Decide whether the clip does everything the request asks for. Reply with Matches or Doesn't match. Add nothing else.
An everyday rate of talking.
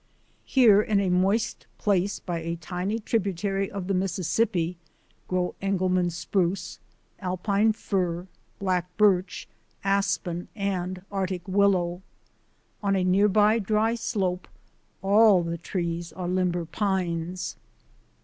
Doesn't match